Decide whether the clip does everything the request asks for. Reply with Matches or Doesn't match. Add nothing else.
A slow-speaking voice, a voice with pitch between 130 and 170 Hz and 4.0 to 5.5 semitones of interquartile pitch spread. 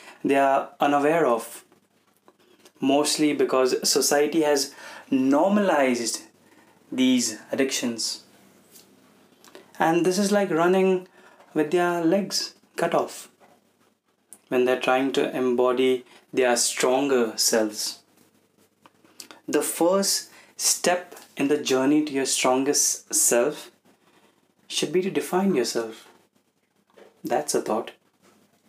Matches